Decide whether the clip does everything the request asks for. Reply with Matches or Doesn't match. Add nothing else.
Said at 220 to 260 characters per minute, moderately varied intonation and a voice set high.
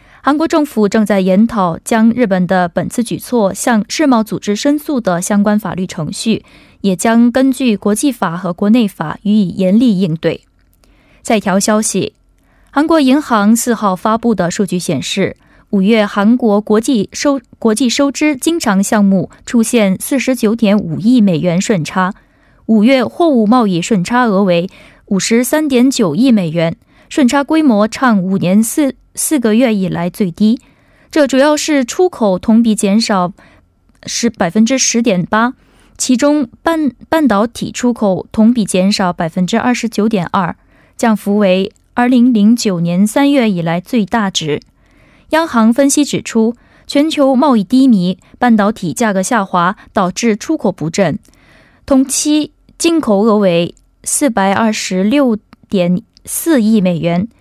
Matches